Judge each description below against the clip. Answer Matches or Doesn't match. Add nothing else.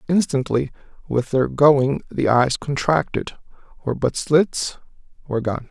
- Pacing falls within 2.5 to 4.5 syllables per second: Matches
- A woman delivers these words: Doesn't match